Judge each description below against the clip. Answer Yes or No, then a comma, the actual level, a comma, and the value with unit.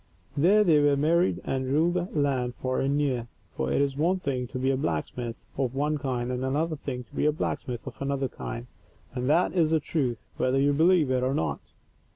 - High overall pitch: No, medium, 140 Hz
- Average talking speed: No, fast, 215 wpm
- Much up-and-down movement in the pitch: No, average, 3.2 semitones